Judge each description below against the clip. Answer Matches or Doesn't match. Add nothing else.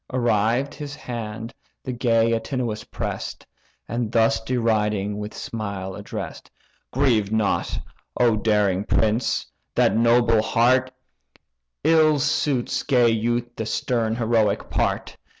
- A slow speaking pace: Matches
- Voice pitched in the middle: Doesn't match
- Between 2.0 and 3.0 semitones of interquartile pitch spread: Matches